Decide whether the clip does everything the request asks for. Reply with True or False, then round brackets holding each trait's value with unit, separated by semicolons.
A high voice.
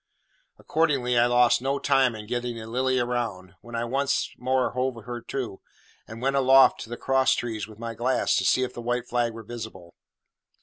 False (120 Hz)